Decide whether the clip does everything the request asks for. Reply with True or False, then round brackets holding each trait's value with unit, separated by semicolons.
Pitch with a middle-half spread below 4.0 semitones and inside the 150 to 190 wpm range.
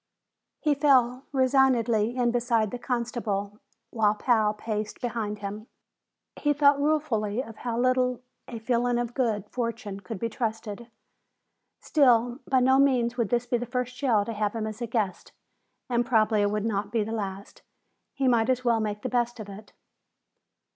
True (2.8 semitones; 170 wpm)